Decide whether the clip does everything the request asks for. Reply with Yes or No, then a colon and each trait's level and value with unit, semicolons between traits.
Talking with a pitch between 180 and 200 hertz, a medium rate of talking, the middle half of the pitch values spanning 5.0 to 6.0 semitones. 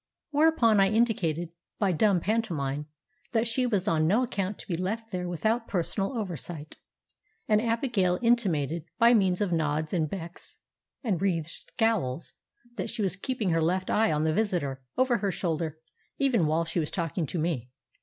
Yes: medium, 185 Hz; average, 170 wpm; wide, 5.4 semitones